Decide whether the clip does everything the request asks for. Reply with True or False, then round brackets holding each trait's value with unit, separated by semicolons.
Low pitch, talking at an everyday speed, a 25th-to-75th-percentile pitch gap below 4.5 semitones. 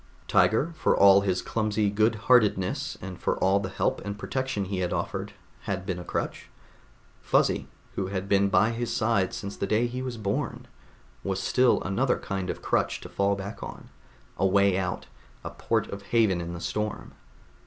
True (100 Hz; 185 wpm; 2.9 semitones)